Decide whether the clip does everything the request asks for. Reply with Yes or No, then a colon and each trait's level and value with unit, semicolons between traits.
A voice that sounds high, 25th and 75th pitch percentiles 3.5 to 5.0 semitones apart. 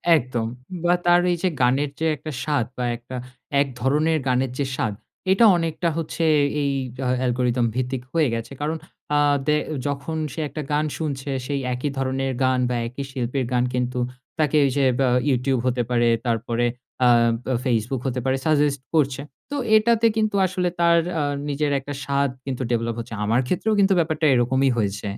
No: low, 135 Hz; average, 3.8 semitones